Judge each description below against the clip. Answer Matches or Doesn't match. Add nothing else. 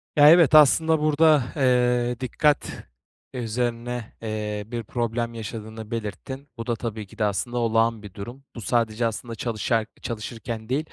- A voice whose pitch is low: Matches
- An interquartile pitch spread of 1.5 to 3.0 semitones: Matches